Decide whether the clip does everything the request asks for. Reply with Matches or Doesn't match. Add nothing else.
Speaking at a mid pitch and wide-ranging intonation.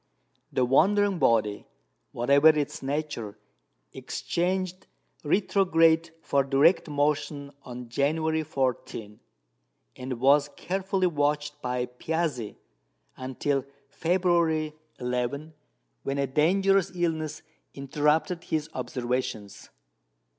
Doesn't match